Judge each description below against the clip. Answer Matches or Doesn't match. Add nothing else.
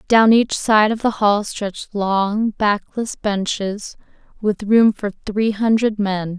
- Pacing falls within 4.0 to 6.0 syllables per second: Doesn't match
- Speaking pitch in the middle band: Doesn't match